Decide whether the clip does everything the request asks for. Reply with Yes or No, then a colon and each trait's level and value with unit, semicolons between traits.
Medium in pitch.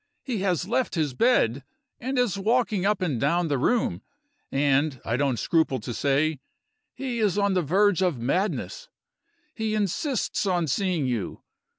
Yes: medium, 180 Hz